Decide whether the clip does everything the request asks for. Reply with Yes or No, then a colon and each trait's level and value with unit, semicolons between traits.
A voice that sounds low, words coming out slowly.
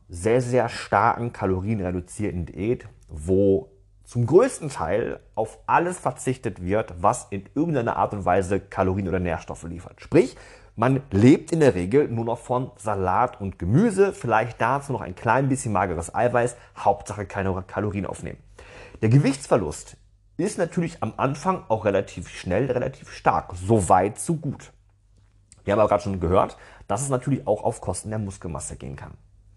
No: low, 105 Hz; average, 160 wpm